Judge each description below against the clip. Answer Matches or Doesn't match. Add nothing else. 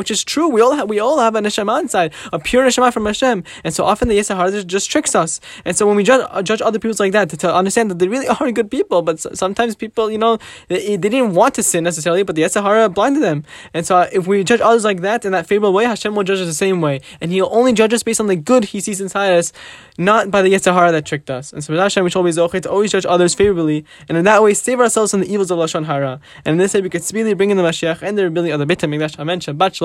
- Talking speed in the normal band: Doesn't match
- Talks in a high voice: Matches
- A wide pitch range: Doesn't match